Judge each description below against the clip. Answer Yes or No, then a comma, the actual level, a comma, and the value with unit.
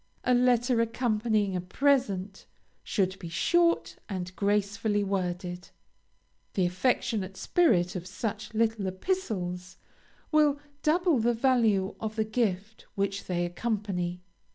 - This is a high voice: Yes, high, 210 Hz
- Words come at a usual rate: No, slow, 115 wpm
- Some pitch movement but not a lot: Yes, average, 4.4 semitones